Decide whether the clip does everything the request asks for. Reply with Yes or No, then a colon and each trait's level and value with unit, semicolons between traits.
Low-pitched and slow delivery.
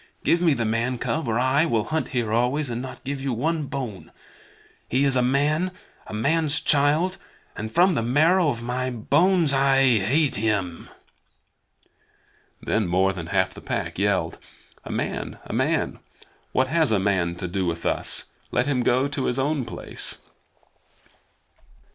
No: low, 130 Hz; average, 165 wpm